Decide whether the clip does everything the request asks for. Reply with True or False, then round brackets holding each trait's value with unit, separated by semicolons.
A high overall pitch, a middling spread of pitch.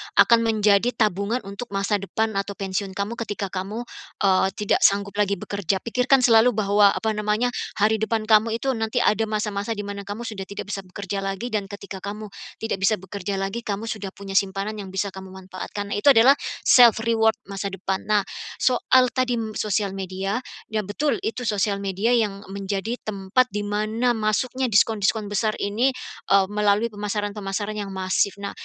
False (205 Hz; 2.0 semitones)